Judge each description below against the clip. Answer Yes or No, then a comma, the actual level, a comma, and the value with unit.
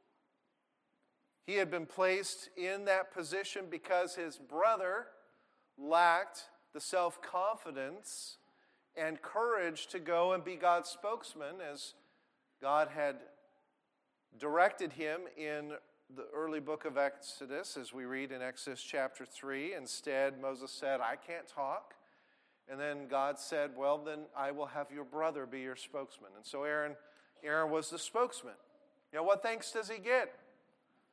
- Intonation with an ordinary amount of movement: No, wide, 5.8 semitones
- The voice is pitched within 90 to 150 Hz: No, medium, 160 Hz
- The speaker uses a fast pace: No, average, 140 wpm